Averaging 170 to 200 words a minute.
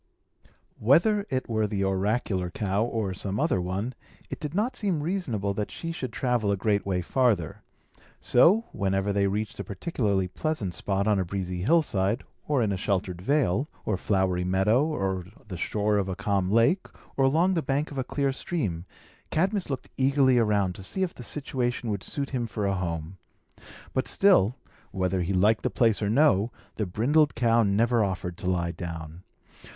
Yes: average, 180 wpm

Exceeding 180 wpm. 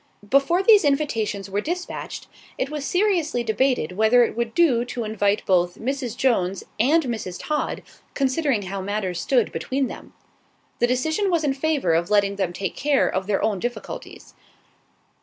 No: average, 160 wpm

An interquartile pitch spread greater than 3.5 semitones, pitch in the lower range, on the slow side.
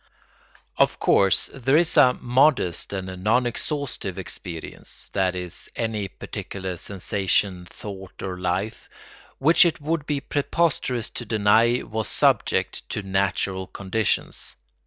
Yes: average, 5.2 semitones; low, 105 Hz; slow, 115 wpm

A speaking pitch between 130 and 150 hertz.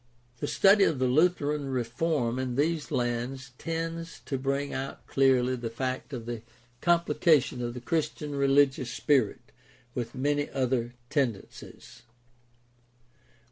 Yes: low, 135 Hz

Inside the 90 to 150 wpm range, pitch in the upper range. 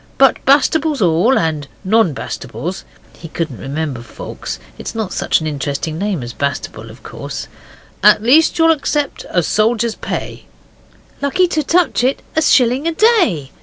No: average, 160 wpm; high, 215 Hz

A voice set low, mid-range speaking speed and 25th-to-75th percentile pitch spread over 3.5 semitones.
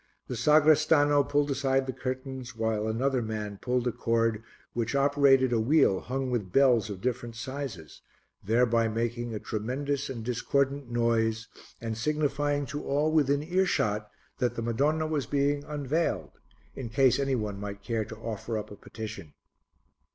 Yes: low, 125 Hz; average, 155 wpm; average, 3.9 semitones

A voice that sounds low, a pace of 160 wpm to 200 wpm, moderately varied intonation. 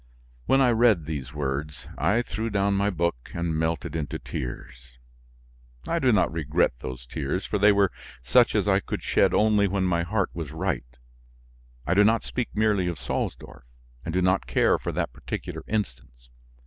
No: very low, 85 Hz; average, 175 wpm; wide, 6.3 semitones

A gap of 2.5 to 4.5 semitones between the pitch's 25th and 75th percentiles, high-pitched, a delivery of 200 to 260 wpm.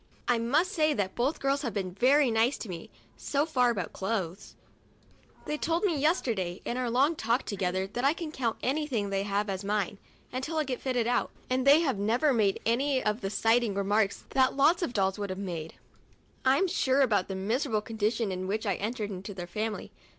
No: wide, 5.4 semitones; high, 230 Hz; fast, 205 wpm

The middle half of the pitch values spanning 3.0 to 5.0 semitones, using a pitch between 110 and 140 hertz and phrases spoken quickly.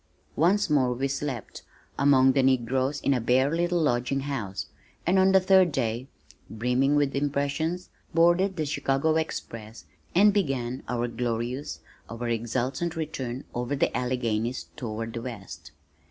No: average, 4.4 semitones; low, 135 Hz; average, 140 wpm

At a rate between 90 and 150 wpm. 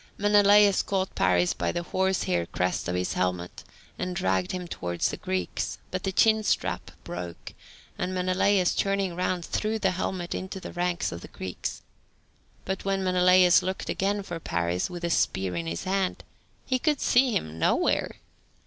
No: average, 165 wpm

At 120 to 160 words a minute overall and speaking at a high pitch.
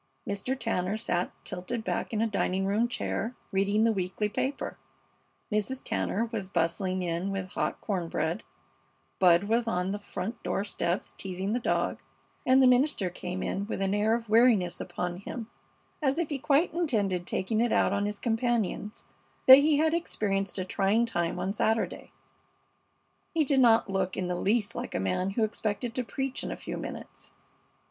No: average, 180 wpm; high, 210 Hz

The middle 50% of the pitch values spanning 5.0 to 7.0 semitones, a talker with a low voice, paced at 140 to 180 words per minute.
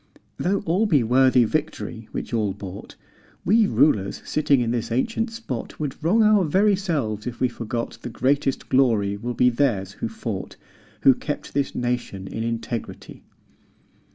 Yes: wide, 5.4 semitones; low, 125 Hz; average, 155 wpm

